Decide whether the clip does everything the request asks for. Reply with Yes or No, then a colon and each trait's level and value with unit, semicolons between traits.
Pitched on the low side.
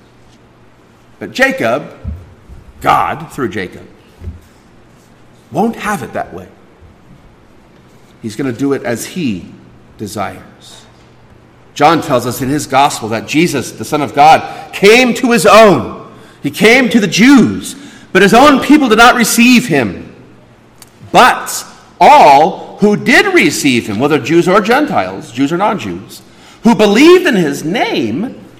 No: high, 205 Hz